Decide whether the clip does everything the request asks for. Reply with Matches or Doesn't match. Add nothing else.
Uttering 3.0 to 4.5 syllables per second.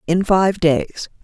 Matches